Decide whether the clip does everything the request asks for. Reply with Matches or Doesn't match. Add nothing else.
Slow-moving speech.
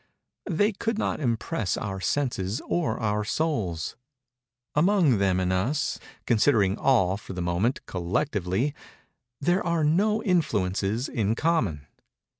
Matches